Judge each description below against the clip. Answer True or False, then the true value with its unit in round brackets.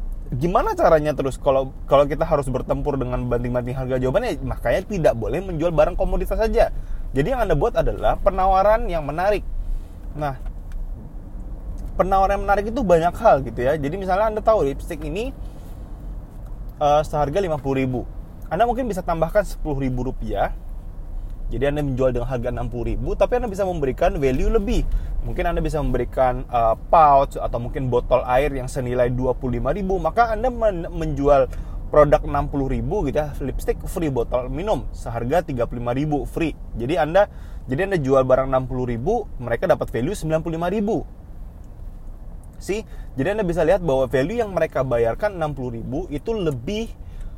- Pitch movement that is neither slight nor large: False (6.1 semitones)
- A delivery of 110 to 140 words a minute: False (160 wpm)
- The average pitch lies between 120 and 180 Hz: True (140 Hz)